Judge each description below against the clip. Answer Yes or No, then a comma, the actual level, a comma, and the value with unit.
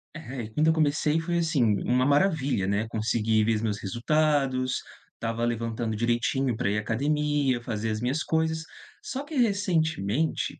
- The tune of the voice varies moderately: No, wide, 5.7 semitones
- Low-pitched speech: Yes, low, 130 Hz